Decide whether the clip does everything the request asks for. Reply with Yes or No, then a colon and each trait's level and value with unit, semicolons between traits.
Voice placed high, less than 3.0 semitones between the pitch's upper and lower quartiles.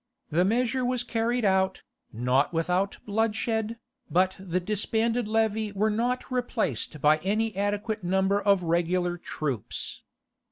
No: high, 205 Hz; average, 4.0 semitones